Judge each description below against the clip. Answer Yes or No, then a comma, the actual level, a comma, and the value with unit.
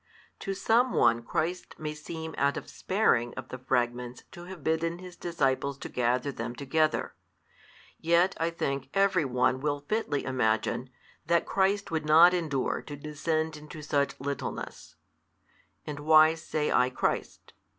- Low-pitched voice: No, medium, 150 Hz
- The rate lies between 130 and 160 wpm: Yes, average, 150 wpm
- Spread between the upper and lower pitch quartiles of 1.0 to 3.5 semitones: No, average, 4.3 semitones